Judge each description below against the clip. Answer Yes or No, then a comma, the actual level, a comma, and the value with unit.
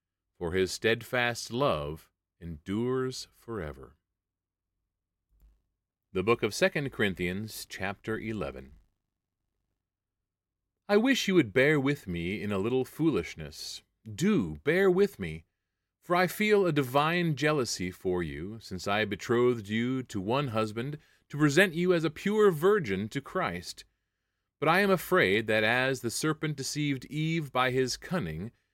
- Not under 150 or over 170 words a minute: No, slow, 135 wpm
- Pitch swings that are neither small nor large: No, wide, 7.7 semitones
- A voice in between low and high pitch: No, low, 110 Hz